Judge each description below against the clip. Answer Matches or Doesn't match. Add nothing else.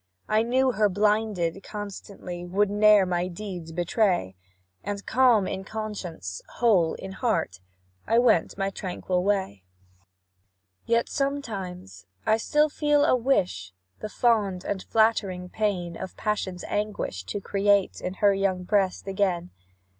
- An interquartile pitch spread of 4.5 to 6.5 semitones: Doesn't match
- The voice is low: Doesn't match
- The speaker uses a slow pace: Matches